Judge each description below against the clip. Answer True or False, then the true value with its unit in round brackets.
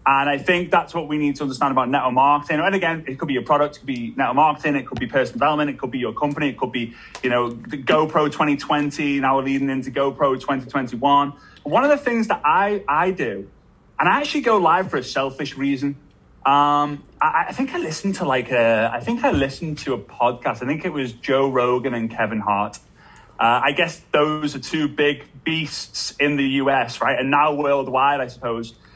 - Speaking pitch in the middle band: True (145 Hz)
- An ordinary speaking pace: False (220 wpm)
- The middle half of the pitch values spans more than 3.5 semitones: False (2.6 semitones)